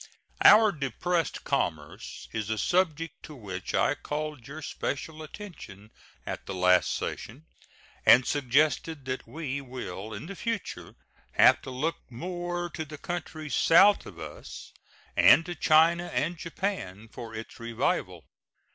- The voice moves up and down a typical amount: No, wide, 6.3 semitones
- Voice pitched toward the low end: No, medium, 150 Hz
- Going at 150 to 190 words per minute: No, average, 140 wpm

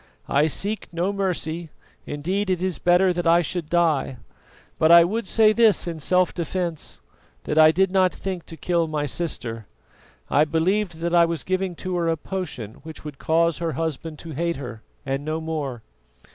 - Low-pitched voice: No, medium, 170 Hz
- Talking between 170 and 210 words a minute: Yes, average, 185 wpm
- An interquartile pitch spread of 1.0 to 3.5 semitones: Yes, average, 2.8 semitones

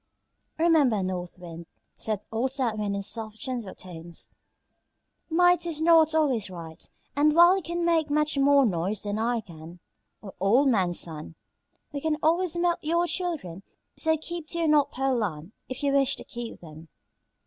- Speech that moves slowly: No, average, 170 wpm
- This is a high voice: Yes, very high, 260 Hz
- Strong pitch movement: Yes, wide, 8.8 semitones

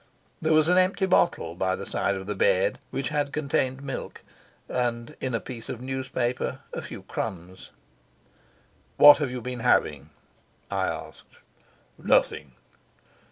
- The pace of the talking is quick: No, average, 145 wpm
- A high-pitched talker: No, low, 125 Hz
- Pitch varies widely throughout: Yes, wide, 6.0 semitones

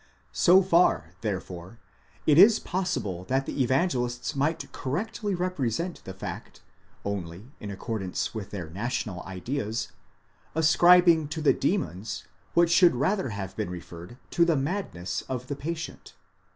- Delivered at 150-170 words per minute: No, average, 140 wpm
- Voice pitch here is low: Yes, low, 130 Hz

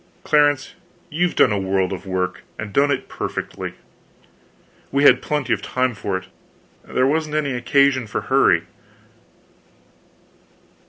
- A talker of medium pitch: No, low, 130 Hz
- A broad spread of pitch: Yes, wide, 6.3 semitones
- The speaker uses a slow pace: Yes, slow, 130 wpm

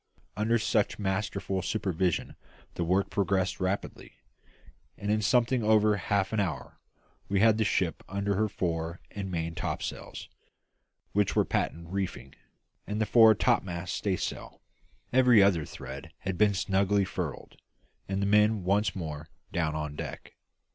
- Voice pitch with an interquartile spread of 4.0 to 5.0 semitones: No, average, 3.1 semitones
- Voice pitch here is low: Yes, low, 100 Hz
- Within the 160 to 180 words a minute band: No, average, 140 wpm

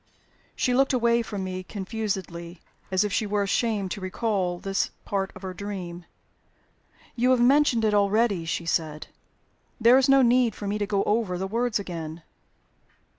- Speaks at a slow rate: No, average, 170 wpm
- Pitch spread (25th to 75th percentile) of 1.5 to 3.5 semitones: No, average, 3.9 semitones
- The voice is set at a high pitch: Yes, high, 205 Hz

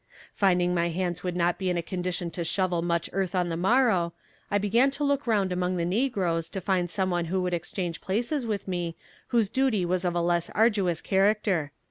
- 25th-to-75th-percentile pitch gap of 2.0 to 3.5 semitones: Yes, average, 2.8 semitones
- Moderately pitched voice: Yes, medium, 180 Hz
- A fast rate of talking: Yes, fast, 210 wpm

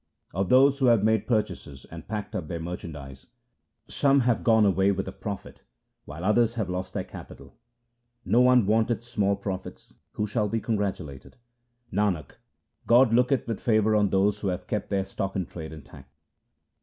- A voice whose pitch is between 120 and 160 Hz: No, low, 105 Hz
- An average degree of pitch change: Yes, average, 3.8 semitones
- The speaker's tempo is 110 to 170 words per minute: No, average, 180 wpm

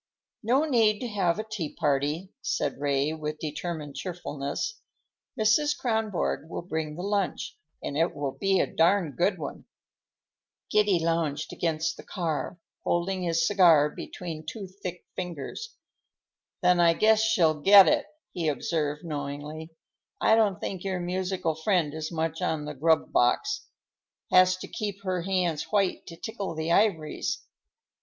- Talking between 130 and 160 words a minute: Yes, average, 150 wpm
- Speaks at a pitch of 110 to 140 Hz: No, medium, 175 Hz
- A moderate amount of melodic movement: Yes, average, 4.1 semitones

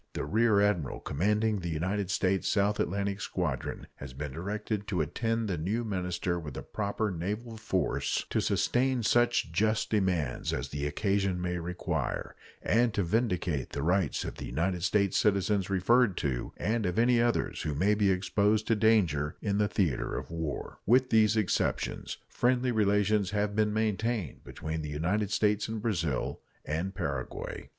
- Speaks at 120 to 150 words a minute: No, average, 165 wpm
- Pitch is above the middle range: No, low, 100 Hz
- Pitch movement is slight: No, average, 3.9 semitones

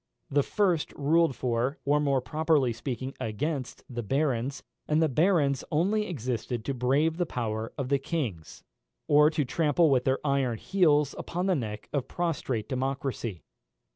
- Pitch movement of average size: Yes, average, 3.9 semitones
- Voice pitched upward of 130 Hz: Yes, medium, 140 Hz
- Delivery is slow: No, average, 155 wpm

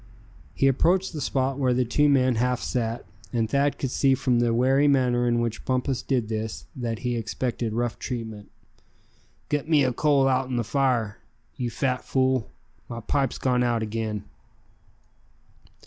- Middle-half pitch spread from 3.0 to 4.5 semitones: No, narrow, 2.5 semitones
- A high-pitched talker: No, low, 125 Hz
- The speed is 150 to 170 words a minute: Yes, average, 165 wpm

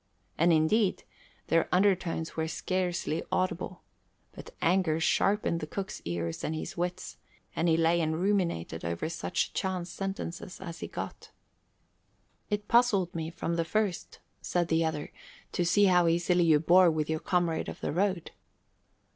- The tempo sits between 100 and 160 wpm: Yes, average, 155 wpm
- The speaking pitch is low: No, medium, 170 Hz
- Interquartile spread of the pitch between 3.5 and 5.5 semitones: No, narrow, 2.5 semitones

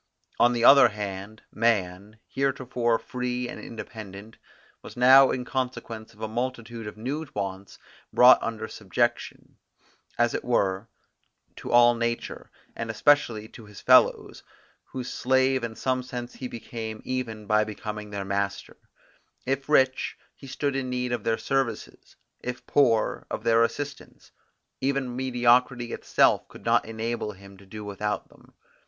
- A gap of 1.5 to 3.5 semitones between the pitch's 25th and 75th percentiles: Yes, average, 2.9 semitones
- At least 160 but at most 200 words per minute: No, average, 145 wpm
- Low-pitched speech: Yes, low, 115 Hz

